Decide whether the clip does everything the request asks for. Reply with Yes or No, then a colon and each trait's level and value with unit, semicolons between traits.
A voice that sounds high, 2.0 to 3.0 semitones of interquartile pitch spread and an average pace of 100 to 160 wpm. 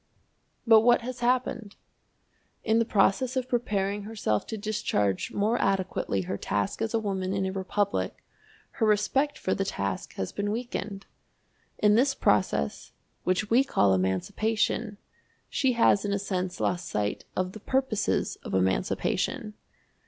No: high, 205 Hz; average, 3.6 semitones; average, 145 wpm